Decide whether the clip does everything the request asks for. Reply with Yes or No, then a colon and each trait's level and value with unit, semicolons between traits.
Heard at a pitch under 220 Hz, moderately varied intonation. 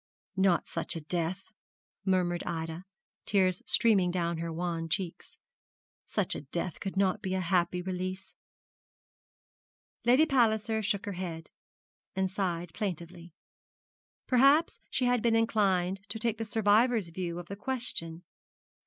Yes: medium, 185 Hz; average, 3.8 semitones